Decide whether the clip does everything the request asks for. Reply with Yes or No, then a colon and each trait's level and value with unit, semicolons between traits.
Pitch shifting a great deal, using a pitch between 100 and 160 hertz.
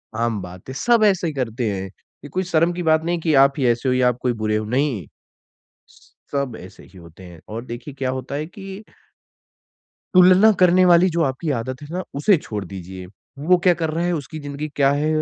Yes: wide, 6.7 semitones; medium, 140 Hz